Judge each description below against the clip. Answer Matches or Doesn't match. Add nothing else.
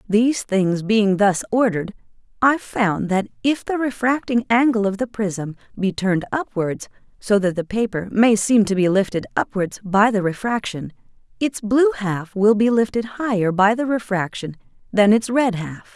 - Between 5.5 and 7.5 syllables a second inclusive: Doesn't match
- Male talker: Doesn't match